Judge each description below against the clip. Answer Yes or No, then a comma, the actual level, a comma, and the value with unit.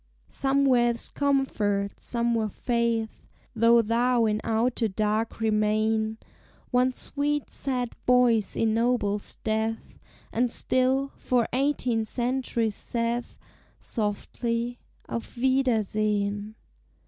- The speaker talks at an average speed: No, slow, 90 wpm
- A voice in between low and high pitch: No, high, 230 Hz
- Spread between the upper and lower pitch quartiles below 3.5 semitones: Yes, narrow, 2.4 semitones